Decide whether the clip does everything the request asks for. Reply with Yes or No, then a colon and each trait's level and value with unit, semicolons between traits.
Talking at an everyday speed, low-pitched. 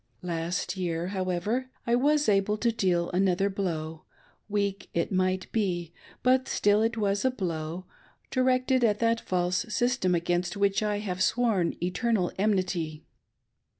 No: average, 150 wpm; high, 195 Hz